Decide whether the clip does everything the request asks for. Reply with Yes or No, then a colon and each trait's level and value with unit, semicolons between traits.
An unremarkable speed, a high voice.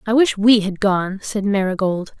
Yes: average, 190 wpm; high, 205 Hz